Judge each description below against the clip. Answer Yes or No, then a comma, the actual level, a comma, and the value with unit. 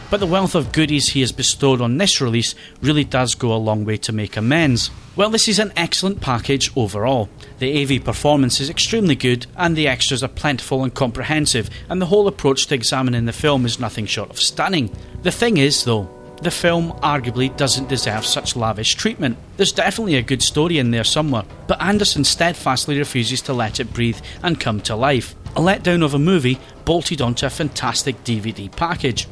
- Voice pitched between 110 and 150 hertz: Yes, low, 135 Hz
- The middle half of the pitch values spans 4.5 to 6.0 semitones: Yes, average, 4.8 semitones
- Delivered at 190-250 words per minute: Yes, average, 195 wpm